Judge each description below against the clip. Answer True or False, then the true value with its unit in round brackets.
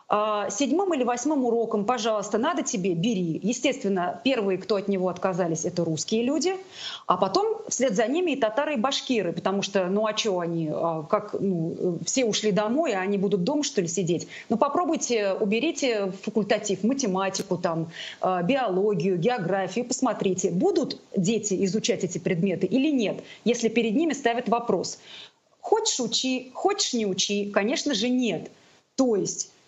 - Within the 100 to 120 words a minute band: False (155 wpm)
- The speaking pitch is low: False (220 Hz)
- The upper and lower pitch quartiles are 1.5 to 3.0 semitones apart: False (5.0 semitones)